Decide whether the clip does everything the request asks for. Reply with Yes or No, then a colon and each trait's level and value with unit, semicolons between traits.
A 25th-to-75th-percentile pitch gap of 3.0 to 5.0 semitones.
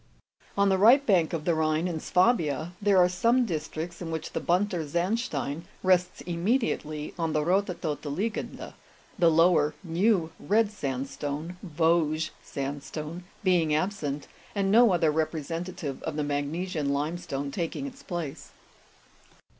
Yes: average, 3.6 semitones